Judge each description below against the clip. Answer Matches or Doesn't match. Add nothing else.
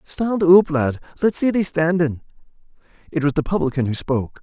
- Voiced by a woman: Doesn't match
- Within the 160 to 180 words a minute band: Matches